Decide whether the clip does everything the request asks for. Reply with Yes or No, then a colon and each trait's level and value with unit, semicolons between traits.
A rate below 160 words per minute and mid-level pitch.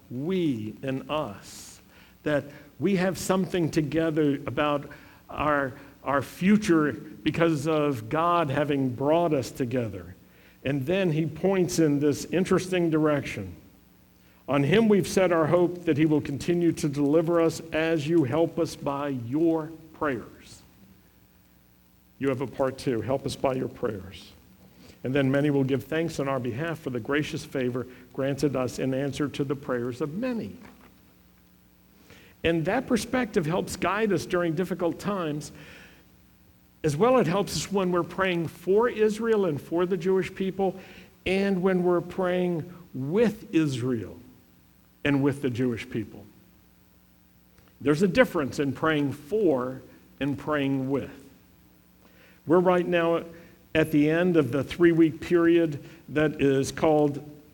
Yes: average, 145 wpm; medium, 155 Hz